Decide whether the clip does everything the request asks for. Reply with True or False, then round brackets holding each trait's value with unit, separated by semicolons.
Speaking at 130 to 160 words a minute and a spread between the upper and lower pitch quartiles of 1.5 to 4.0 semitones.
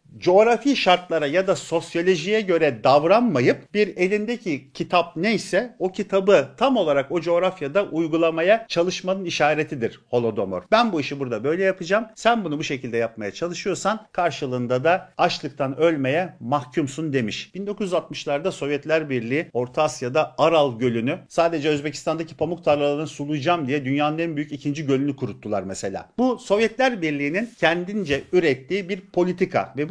False (135 wpm; 4.6 semitones)